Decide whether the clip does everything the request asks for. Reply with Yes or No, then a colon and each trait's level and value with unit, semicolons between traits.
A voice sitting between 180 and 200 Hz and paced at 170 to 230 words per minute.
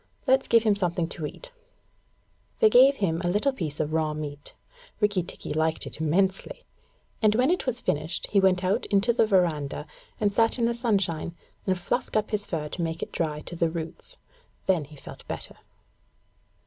Yes: medium, 185 Hz; average, 185 wpm